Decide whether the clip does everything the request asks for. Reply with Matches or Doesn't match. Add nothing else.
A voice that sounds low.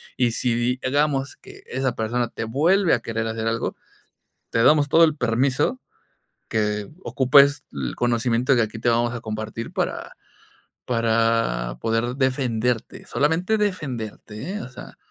Matches